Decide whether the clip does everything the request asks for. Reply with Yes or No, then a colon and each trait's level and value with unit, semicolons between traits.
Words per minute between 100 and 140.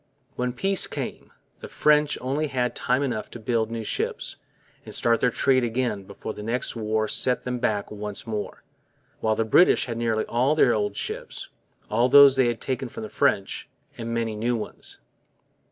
No: average, 185 wpm